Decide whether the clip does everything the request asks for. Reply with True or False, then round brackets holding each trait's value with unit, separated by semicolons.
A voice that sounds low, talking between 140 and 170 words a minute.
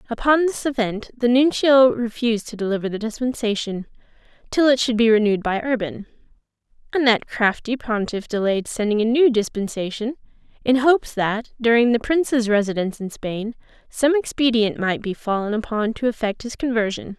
False (230 Hz; 155 wpm)